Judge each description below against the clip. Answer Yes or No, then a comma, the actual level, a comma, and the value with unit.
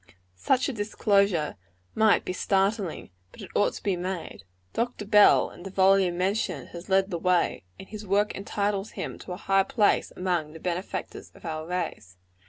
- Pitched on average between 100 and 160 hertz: No, high, 190 Hz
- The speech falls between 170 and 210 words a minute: Yes, average, 180 wpm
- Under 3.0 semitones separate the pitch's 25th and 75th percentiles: Yes, narrow, 2.6 semitones